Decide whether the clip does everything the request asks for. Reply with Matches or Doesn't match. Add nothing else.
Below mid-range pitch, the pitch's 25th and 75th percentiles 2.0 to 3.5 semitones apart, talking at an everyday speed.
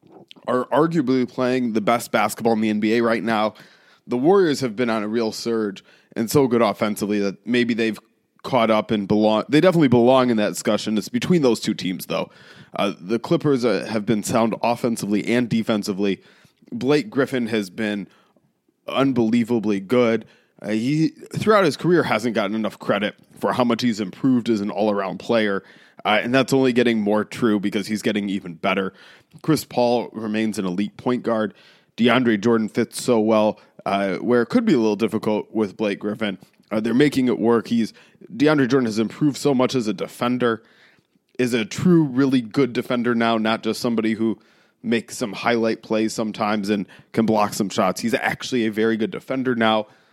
Matches